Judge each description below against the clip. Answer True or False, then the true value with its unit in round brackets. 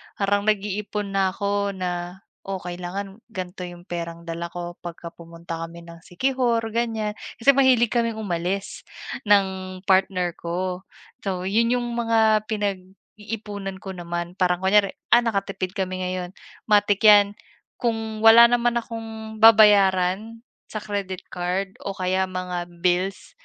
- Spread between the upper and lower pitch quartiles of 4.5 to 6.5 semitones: False (3.1 semitones)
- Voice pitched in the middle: False (195 Hz)